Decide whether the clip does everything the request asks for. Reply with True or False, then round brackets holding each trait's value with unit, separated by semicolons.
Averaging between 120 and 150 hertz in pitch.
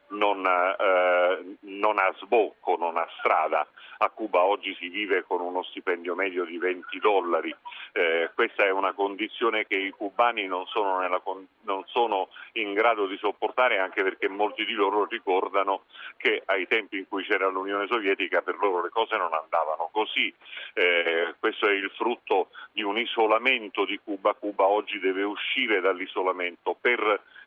False (100 Hz)